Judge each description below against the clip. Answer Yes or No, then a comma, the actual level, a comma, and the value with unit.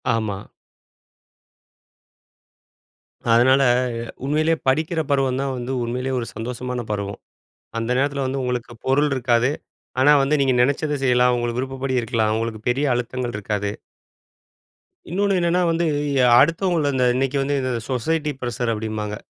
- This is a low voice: Yes, low, 130 Hz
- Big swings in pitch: No, average, 3.1 semitones